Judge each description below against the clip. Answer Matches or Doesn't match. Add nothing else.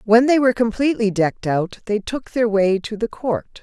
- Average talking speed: Doesn't match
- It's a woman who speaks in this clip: Matches